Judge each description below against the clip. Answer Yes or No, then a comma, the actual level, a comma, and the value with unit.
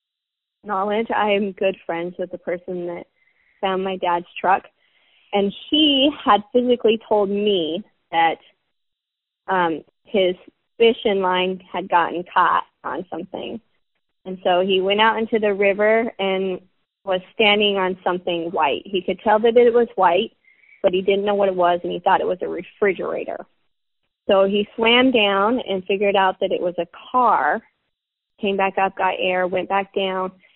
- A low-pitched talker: No, high, 195 Hz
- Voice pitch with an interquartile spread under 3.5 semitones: Yes, average, 3.0 semitones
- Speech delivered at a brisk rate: No, average, 165 wpm